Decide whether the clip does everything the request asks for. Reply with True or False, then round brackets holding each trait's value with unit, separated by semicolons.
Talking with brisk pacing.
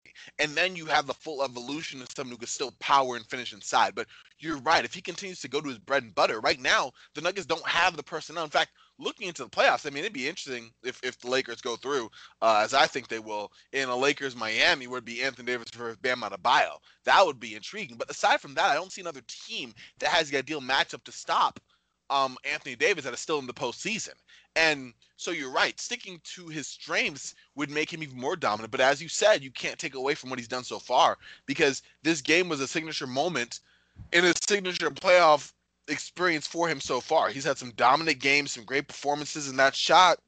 True (235 wpm)